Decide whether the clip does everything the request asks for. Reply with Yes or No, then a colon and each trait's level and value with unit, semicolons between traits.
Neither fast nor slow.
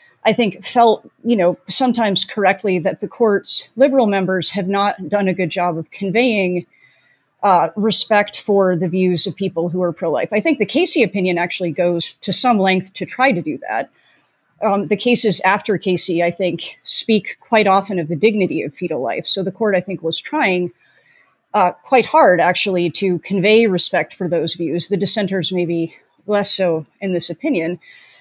Yes: average, 185 wpm